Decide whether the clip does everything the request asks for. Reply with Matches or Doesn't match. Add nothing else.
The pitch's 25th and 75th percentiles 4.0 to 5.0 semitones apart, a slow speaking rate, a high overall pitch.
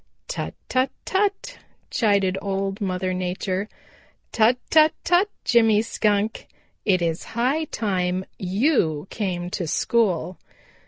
Matches